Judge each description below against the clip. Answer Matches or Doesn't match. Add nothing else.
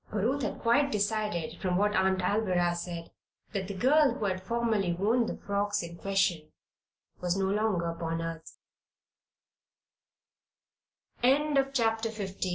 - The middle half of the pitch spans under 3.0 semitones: Doesn't match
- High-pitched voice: Matches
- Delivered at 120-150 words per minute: Matches